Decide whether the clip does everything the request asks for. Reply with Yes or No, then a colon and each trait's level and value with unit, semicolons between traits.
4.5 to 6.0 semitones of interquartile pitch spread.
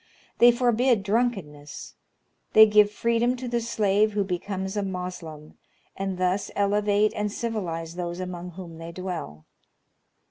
No: average, 3.4 semitones